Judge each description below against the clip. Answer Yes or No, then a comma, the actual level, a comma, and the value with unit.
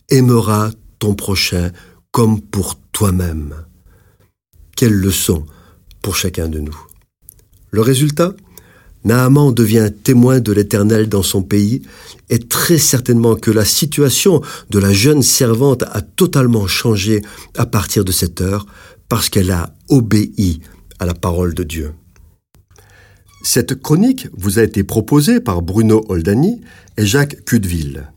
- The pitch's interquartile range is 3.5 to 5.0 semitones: Yes, average, 4.7 semitones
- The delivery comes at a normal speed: No, slow, 130 wpm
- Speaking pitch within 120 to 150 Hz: No, low, 105 Hz